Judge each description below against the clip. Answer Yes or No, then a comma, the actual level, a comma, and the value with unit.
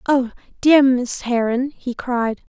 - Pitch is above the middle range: Yes, very high, 250 Hz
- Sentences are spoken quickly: No, average, 140 wpm